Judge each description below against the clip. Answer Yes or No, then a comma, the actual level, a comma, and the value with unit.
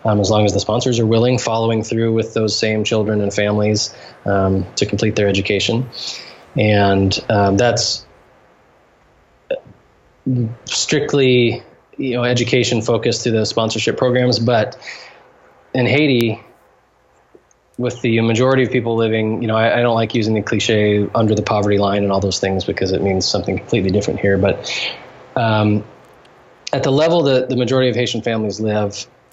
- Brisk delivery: No, average, 160 wpm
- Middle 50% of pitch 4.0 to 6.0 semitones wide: No, average, 2.7 semitones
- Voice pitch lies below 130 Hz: Yes, low, 110 Hz